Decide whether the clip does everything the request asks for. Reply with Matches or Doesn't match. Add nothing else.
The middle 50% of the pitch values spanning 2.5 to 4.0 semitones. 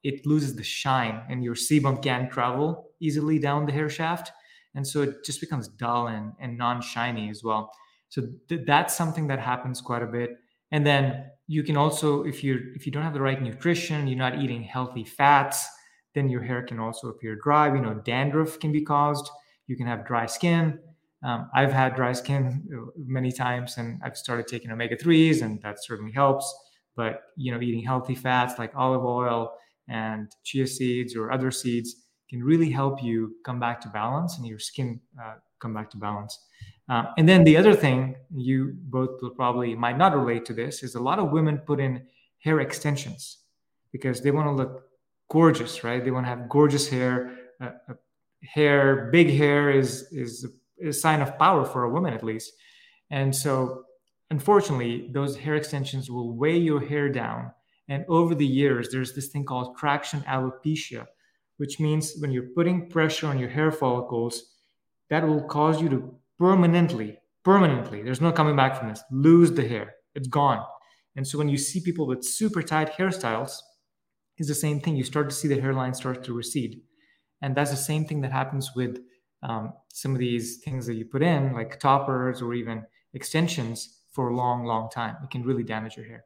Matches